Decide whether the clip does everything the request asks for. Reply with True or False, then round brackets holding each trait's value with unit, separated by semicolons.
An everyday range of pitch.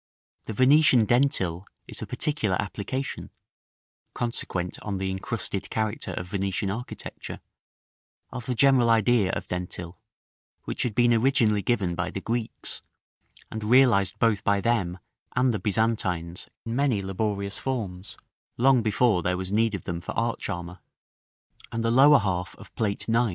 True (4.1 semitones)